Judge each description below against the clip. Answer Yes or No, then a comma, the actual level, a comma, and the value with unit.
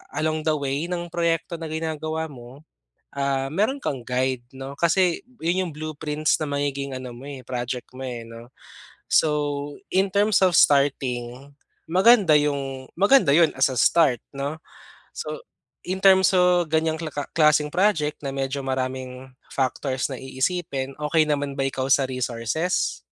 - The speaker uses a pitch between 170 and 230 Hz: No, medium, 145 Hz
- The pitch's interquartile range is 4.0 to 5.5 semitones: No, average, 3.6 semitones